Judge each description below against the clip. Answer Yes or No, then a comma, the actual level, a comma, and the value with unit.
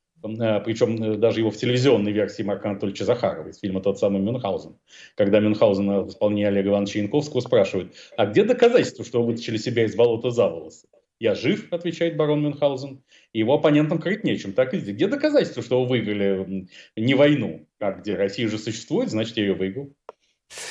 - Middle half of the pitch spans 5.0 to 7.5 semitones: Yes, wide, 5.6 semitones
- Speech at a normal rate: No, fast, 175 wpm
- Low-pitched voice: Yes, low, 115 Hz